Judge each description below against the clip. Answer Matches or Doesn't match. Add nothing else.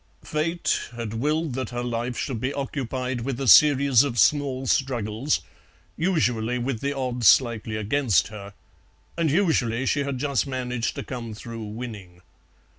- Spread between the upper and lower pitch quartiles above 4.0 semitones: Doesn't match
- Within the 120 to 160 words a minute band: Matches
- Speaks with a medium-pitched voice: Doesn't match